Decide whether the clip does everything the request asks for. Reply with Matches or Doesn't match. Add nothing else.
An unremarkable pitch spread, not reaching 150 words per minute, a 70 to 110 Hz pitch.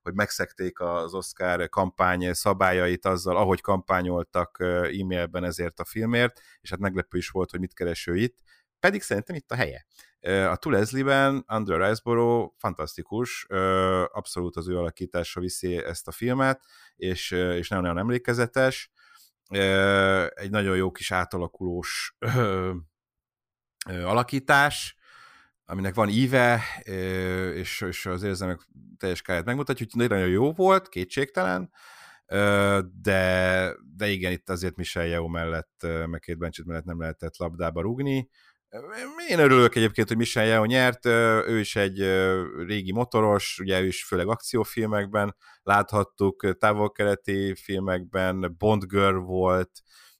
Matches